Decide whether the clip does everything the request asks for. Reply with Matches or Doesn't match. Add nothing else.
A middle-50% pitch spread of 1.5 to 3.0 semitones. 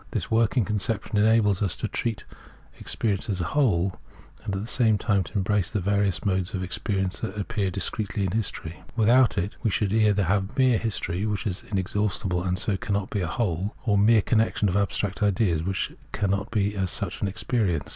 Matches